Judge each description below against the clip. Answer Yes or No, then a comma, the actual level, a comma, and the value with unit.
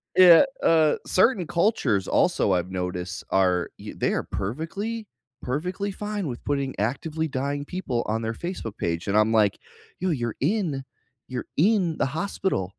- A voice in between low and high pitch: Yes, medium, 145 Hz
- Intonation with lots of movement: Yes, wide, 9.0 semitones